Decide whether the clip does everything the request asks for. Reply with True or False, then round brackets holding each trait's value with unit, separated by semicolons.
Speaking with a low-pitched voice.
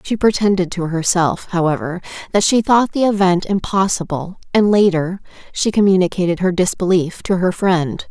False (185 Hz)